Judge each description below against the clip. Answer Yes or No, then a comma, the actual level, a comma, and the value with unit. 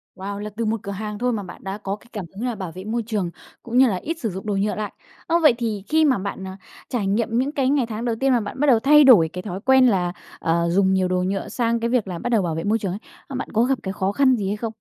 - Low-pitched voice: No, high, 215 Hz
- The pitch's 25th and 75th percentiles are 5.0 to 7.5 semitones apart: No, average, 4.3 semitones